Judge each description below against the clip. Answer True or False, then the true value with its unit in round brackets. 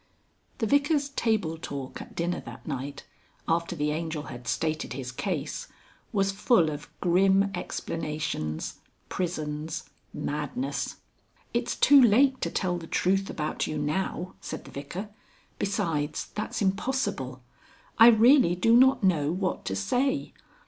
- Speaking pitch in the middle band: True (175 Hz)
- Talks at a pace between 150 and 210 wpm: False (135 wpm)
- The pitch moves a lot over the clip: True (6.1 semitones)